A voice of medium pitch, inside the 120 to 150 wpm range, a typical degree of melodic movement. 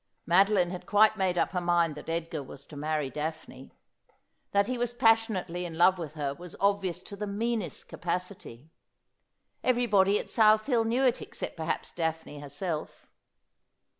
No: medium, 180 Hz; average, 165 wpm; average, 4.7 semitones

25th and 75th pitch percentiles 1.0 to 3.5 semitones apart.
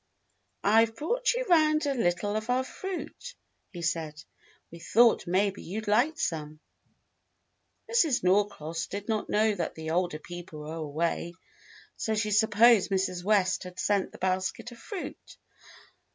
No: average, 5.1 semitones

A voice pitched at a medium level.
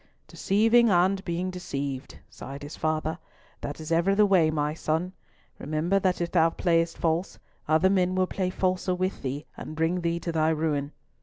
Yes: medium, 170 Hz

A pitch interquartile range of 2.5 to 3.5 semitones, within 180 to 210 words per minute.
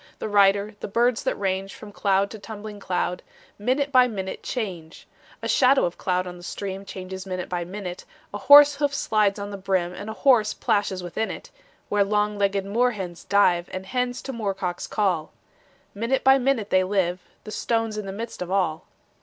Yes: average, 3.0 semitones; average, 195 wpm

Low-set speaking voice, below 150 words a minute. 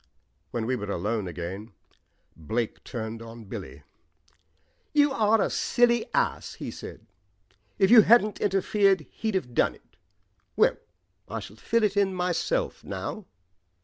No: medium, 180 Hz; average, 140 wpm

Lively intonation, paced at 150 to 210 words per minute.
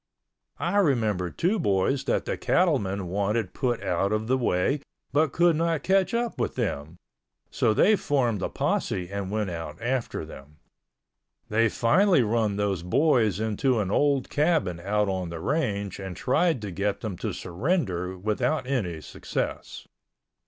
Yes: wide, 7.1 semitones; average, 155 wpm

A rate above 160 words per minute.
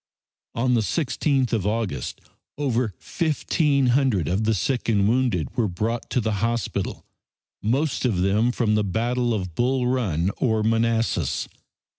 No: average, 145 wpm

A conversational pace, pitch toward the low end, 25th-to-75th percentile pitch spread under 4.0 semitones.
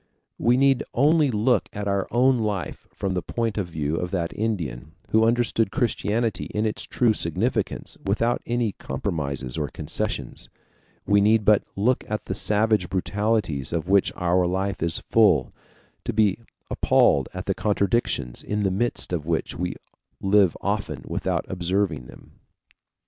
No: average, 150 wpm; low, 100 Hz; average, 4.3 semitones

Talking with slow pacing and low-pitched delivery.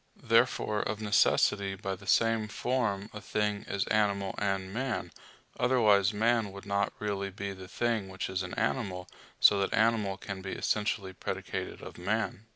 No: average, 160 wpm; low, 100 Hz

